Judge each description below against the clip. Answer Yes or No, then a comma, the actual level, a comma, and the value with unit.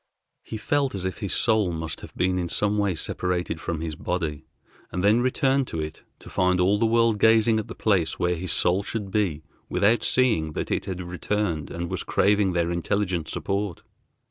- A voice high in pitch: No, very low, 95 Hz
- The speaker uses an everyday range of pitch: Yes, average, 3.6 semitones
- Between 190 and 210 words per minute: Yes, average, 195 wpm